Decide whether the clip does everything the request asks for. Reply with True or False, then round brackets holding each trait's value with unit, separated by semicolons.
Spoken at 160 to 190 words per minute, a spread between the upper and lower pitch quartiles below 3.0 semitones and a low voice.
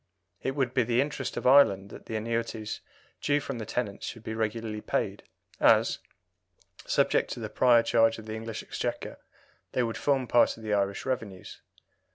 True (180 wpm; 2.6 semitones; 115 Hz)